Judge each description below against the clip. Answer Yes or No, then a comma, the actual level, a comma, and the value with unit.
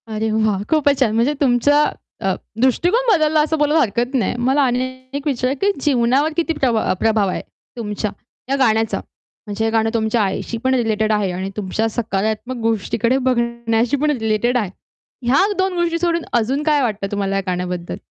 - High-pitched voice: Yes, high, 235 Hz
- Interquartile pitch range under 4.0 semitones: No, average, 4.6 semitones